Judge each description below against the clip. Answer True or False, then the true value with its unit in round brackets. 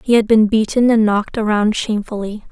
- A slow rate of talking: False (190 wpm)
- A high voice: True (215 Hz)